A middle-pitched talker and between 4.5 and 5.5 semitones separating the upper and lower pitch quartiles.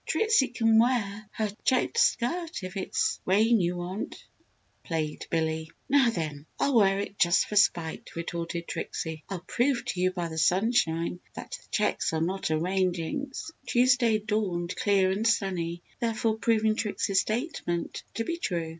No: high, 195 Hz; average, 4.9 semitones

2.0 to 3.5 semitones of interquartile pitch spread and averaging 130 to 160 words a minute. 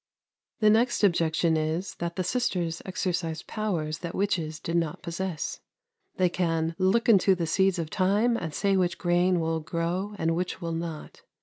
No: narrow, 2.6 semitones; average, 170 wpm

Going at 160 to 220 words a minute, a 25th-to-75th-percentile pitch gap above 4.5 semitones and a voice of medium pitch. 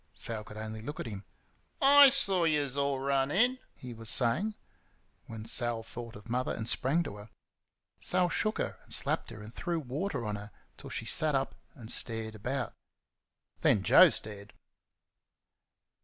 No: average, 170 wpm; wide, 5.5 semitones; low, 120 Hz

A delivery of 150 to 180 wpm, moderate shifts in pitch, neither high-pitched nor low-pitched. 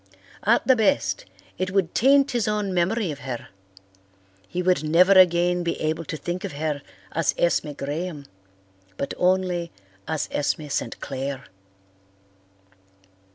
No: slow, 135 wpm; average, 3.8 semitones; medium, 175 Hz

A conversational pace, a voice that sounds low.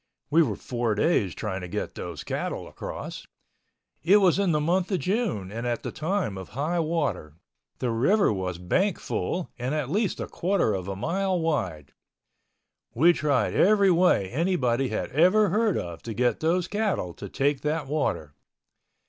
No: average, 170 wpm; medium, 150 Hz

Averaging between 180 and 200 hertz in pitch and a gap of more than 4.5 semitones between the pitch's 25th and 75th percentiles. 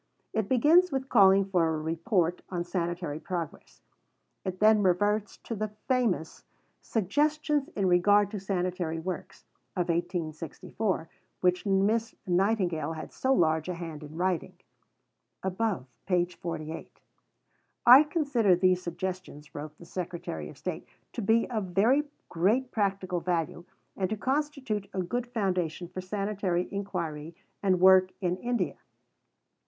No: medium, 185 Hz; average, 3.8 semitones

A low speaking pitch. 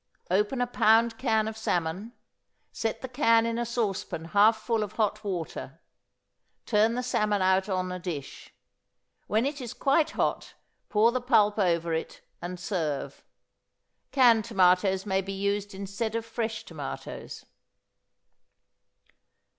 No: high, 210 Hz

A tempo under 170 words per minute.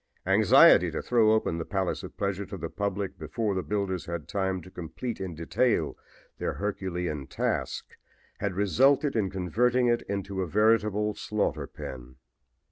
Yes: average, 155 wpm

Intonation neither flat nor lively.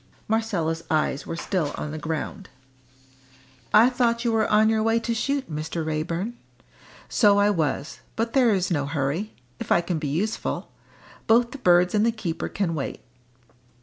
No: wide, 5.8 semitones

